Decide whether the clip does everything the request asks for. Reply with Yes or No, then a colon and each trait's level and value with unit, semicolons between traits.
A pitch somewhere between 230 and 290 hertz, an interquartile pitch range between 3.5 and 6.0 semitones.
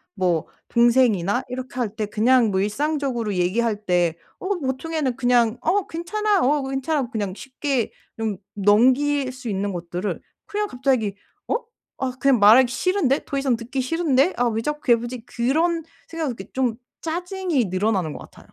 Yes: very high, 250 Hz; average, 5.3 semitones